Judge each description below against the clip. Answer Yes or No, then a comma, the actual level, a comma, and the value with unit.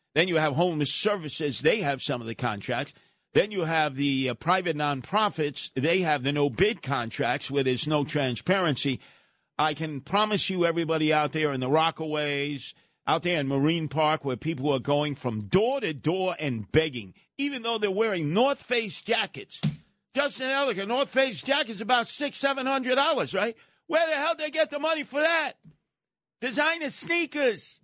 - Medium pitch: Yes, medium, 160 Hz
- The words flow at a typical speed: Yes, average, 180 wpm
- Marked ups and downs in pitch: Yes, wide, 8.7 semitones